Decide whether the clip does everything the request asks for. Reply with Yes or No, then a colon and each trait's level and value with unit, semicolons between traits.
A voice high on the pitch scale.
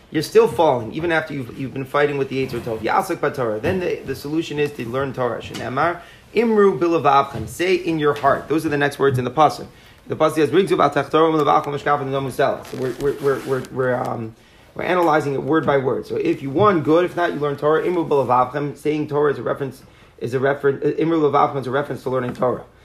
No: medium, 145 Hz